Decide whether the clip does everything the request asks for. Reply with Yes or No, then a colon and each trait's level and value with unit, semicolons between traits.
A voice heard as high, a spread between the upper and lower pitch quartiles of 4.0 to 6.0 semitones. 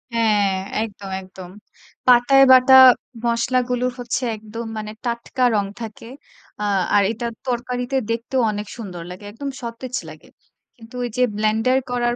No: high, 235 Hz; average, 2.8 semitones